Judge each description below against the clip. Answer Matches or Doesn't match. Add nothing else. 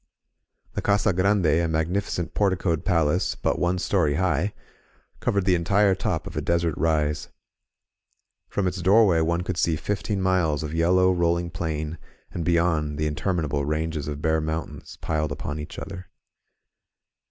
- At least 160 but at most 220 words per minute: Doesn't match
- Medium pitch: Doesn't match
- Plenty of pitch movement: Doesn't match